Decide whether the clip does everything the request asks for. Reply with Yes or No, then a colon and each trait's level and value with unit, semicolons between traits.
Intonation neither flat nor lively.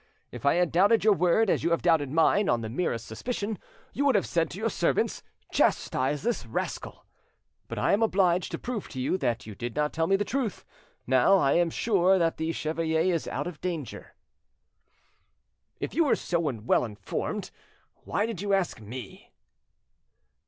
No: wide, 6.0 semitones